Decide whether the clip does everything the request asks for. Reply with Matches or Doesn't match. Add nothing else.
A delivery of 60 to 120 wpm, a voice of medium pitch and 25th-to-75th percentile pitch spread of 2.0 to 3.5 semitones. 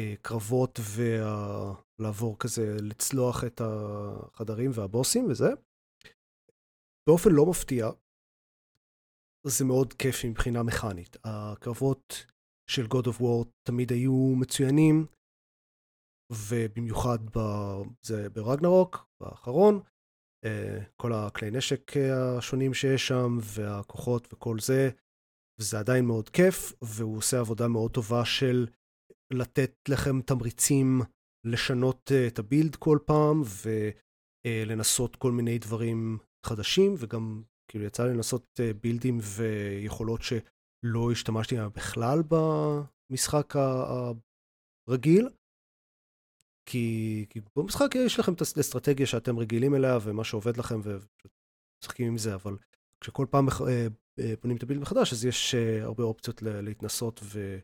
Doesn't match